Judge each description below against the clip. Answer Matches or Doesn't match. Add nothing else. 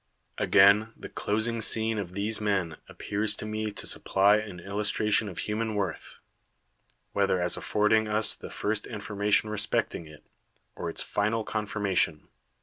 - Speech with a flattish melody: Matches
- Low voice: Matches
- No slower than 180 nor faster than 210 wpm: Doesn't match